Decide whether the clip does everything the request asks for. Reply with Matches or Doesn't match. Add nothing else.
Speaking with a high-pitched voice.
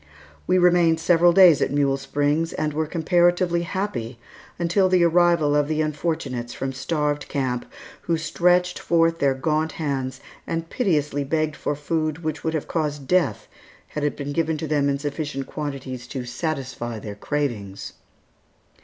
Doesn't match